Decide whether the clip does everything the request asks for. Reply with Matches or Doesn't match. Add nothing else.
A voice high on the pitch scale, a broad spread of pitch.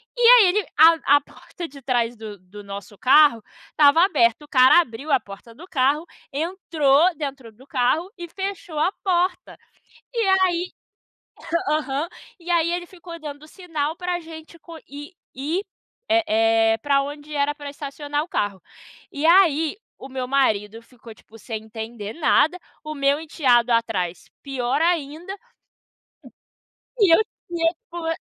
Matches